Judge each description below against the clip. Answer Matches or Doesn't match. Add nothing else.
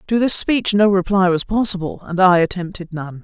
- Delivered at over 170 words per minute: Matches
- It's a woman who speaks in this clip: Matches